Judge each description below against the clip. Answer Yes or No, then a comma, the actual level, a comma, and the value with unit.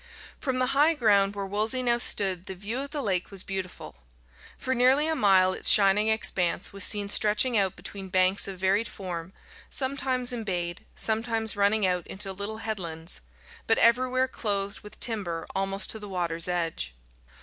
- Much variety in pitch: No, average, 3.7 semitones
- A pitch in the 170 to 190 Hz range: No, high, 200 Hz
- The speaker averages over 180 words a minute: No, average, 170 wpm